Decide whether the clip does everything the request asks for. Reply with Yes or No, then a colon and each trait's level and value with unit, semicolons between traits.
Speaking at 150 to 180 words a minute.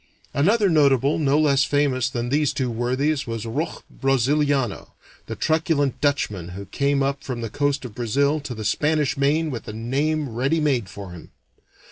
Yes: average, 170 wpm